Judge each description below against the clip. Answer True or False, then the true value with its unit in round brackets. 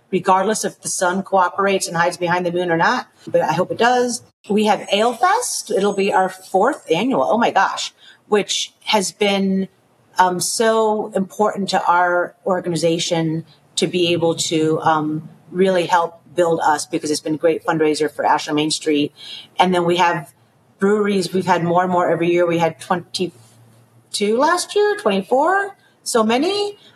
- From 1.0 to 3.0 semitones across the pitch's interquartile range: False (3.6 semitones)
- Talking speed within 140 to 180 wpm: True (170 wpm)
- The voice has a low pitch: False (180 Hz)